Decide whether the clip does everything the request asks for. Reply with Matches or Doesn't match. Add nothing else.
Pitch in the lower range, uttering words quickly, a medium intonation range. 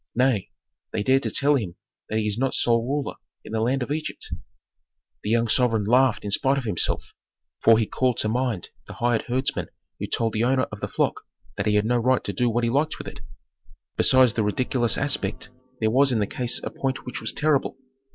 Matches